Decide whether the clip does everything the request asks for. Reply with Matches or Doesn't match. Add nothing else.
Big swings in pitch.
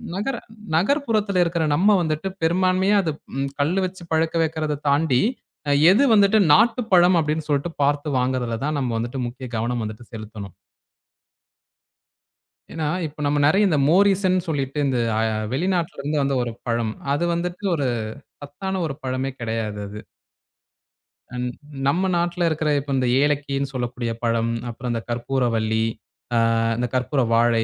Matches